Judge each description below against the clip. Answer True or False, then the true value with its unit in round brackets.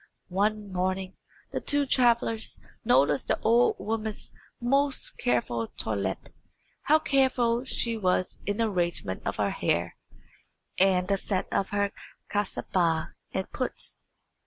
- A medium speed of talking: False (125 wpm)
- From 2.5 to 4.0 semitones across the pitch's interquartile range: False (4.5 semitones)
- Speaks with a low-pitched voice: False (205 Hz)